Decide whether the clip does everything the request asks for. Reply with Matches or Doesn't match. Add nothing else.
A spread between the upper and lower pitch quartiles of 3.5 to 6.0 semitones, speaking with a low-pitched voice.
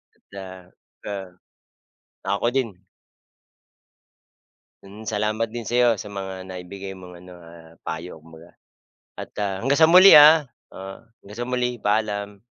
Matches